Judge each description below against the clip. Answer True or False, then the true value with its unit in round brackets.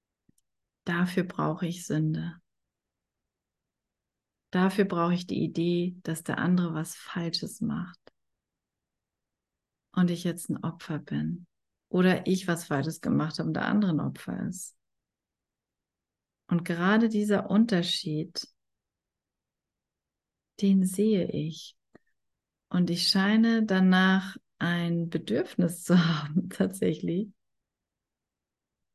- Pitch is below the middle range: False (175 Hz)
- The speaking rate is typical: False (100 wpm)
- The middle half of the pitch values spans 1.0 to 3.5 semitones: True (2.9 semitones)